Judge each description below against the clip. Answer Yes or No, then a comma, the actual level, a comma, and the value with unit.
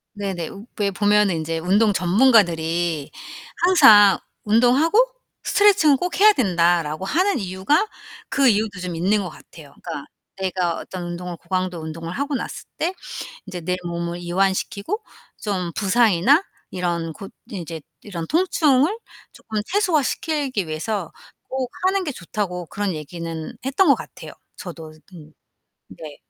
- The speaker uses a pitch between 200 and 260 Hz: No, high, 190 Hz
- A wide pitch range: Yes, wide, 7.3 semitones